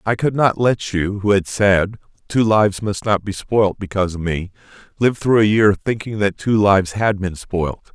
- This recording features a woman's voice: No, male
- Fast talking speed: Yes, fast, 210 wpm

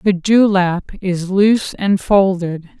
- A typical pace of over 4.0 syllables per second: No, 3.6 syllables/s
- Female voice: Yes, female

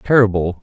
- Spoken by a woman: No, male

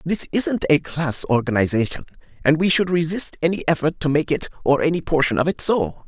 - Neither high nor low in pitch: Yes, medium, 155 Hz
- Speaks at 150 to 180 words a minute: No, average, 200 wpm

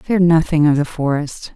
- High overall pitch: No, medium, 155 Hz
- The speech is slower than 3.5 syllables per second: No, 4.6 syllables/s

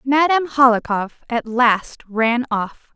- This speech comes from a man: No, female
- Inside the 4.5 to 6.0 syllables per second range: No, 3.6 syllables/s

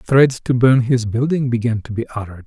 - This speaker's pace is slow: No, fast, 220 wpm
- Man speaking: Yes, male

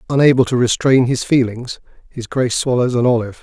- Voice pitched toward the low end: Yes, low, 125 Hz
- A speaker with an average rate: Yes, average, 175 wpm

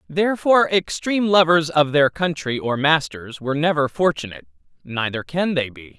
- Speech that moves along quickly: No, average, 150 wpm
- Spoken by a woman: No, male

